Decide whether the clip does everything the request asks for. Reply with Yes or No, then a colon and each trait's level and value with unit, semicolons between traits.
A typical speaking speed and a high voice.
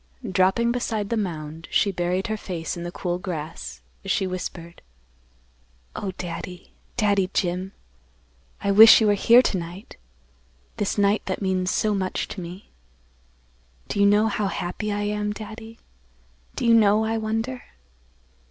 Yes: average, 150 wpm; high, 200 Hz